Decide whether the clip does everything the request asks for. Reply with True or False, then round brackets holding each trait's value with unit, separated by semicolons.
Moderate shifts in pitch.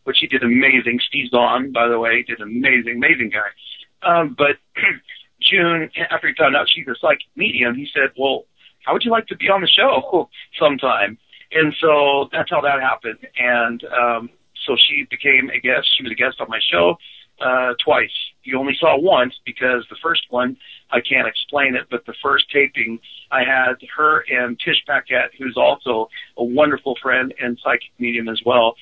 True (3.9 semitones)